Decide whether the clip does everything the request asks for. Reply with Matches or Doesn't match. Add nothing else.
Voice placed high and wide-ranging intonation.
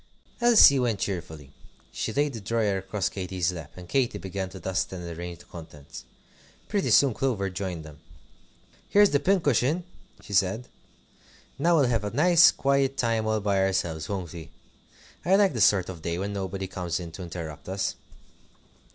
Doesn't match